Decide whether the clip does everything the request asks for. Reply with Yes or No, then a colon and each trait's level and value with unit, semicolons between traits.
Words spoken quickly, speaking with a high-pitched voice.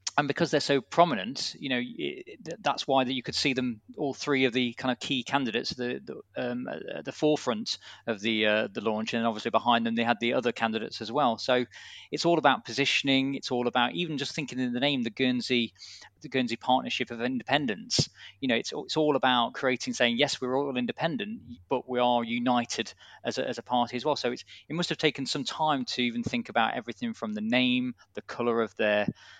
No: fast, 225 wpm; low, 125 Hz